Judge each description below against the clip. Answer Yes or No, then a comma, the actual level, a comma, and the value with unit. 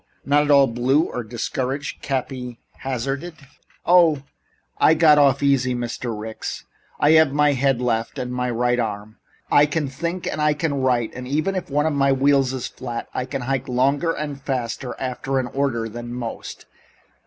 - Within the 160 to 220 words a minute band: Yes, average, 175 wpm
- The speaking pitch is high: No, low, 135 Hz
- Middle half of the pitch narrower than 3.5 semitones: Yes, average, 2.9 semitones